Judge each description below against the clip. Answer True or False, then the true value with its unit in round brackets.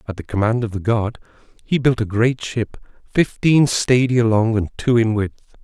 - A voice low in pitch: True (115 Hz)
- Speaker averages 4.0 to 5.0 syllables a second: True (4.7 syllables/s)